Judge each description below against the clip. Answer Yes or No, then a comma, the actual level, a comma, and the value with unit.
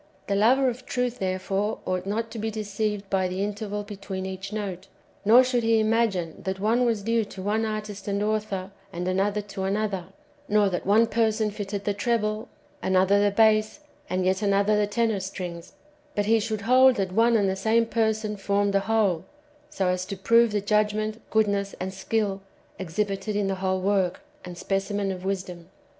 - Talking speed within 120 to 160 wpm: No, average, 185 wpm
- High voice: Yes, high, 205 Hz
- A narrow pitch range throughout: Yes, narrow, 2.2 semitones